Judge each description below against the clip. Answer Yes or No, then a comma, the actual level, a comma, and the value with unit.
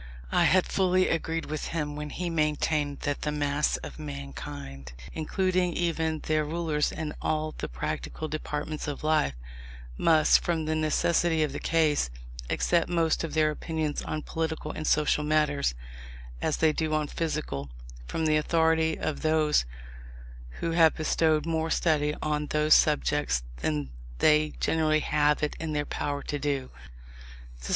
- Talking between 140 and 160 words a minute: Yes, average, 150 wpm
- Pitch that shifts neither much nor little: No, narrow, 1.5 semitones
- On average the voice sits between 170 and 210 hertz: No, medium, 155 Hz